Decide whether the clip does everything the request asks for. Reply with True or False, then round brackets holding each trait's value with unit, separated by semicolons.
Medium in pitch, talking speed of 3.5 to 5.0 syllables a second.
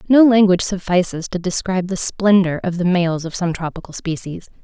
False (180 Hz; 5.5 syllables/s)